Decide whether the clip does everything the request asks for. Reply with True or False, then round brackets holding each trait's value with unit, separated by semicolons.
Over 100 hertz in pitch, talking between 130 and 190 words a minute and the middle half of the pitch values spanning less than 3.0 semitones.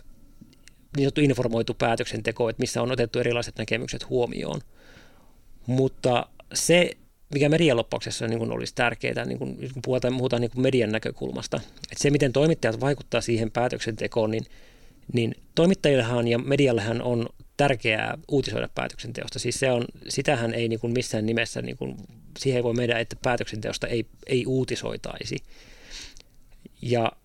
True (120 Hz; 140 wpm; 2.4 semitones)